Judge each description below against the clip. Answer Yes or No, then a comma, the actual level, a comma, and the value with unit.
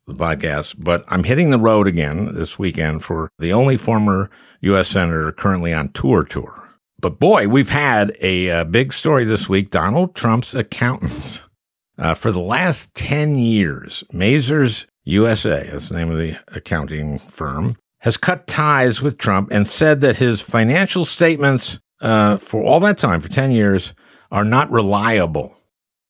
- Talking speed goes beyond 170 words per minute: No, average, 160 wpm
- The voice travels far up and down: Yes, wide, 6.6 semitones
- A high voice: No, low, 105 Hz